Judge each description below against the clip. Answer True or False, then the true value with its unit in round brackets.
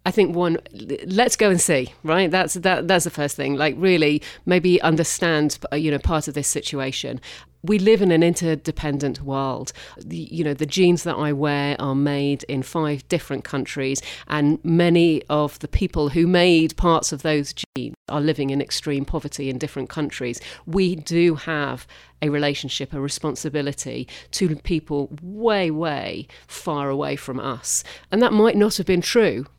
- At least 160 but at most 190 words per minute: True (170 wpm)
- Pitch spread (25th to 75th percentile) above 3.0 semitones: True (3.5 semitones)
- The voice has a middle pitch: True (150 Hz)